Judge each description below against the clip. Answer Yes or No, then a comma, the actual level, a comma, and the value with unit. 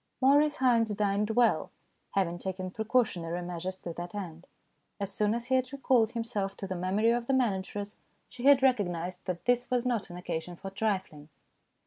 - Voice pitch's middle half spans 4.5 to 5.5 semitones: Yes, average, 4.9 semitones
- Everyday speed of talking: Yes, average, 180 wpm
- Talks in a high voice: Yes, high, 205 Hz